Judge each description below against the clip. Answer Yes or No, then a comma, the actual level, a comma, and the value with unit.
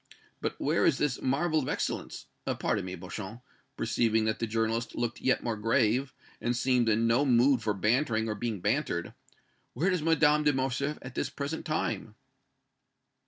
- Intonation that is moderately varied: Yes, average, 4.1 semitones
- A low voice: Yes, low, 120 Hz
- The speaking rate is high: No, average, 165 wpm